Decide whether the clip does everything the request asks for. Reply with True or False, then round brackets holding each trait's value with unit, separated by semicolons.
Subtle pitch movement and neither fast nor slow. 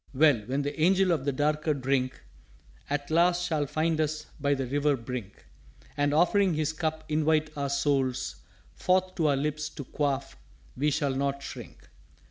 True (2.2 semitones; 165 wpm)